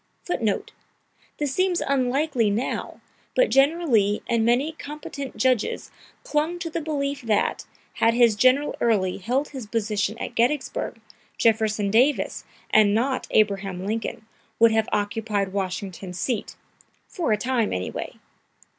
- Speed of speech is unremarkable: No, slow, 130 wpm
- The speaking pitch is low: No, high, 230 Hz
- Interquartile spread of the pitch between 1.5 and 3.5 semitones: No, average, 5.0 semitones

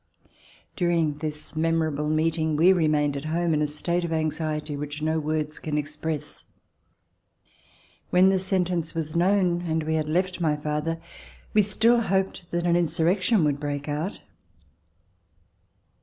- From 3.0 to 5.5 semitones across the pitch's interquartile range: No, narrow, 2.4 semitones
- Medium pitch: Yes, medium, 160 Hz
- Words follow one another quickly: No, average, 140 wpm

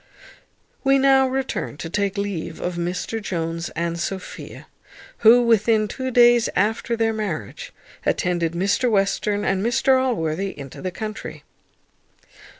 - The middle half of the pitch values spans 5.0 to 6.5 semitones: Yes, average, 5.3 semitones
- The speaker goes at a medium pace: No, slow, 130 wpm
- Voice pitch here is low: No, high, 205 Hz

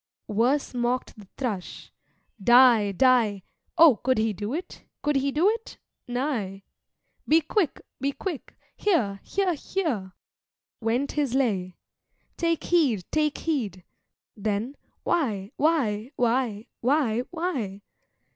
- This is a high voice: Yes, very high, 250 Hz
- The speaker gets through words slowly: Yes, slow, 120 wpm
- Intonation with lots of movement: Yes, wide, 6.3 semitones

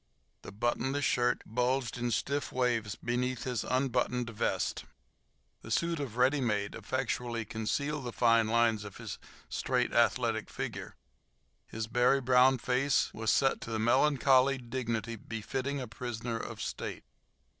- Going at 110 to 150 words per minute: Yes, average, 140 wpm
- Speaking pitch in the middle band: No, low, 125 Hz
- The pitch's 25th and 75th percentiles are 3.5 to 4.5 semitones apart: No, narrow, 2.5 semitones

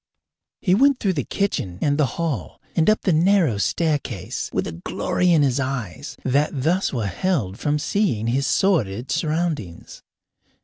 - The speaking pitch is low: No, medium, 145 Hz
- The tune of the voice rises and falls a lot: Yes, wide, 7.0 semitones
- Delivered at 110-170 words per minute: Yes, average, 160 wpm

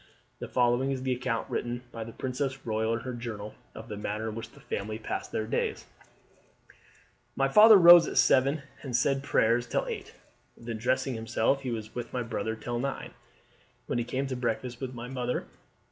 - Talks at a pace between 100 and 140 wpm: No, average, 190 wpm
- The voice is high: No, low, 120 Hz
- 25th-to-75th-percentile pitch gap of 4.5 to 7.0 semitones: No, narrow, 2.6 semitones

